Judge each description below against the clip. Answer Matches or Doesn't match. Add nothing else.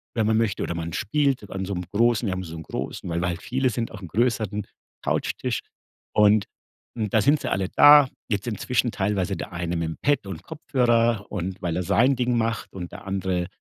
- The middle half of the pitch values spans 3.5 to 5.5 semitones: Matches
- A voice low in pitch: Matches